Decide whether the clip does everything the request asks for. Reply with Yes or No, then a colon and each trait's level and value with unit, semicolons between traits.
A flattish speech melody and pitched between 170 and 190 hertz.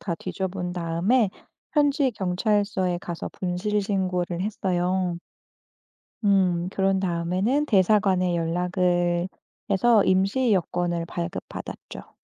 Yes: narrow, 2.3 semitones; medium, 185 Hz